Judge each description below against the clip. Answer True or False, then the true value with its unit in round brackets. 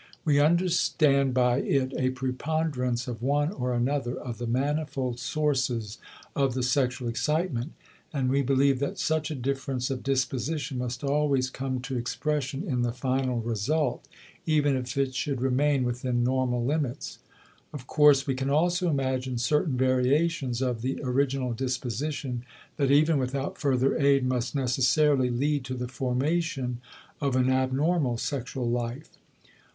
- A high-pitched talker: False (130 Hz)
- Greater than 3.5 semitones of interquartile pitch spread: False (2.5 semitones)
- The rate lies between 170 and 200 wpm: False (145 wpm)